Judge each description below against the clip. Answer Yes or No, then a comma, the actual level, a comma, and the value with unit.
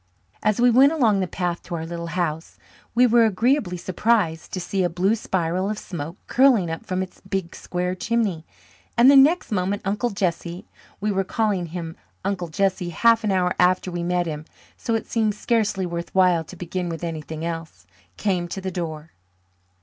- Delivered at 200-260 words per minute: No, average, 185 wpm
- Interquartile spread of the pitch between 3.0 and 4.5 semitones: Yes, average, 3.8 semitones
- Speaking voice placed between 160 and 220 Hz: Yes, medium, 185 Hz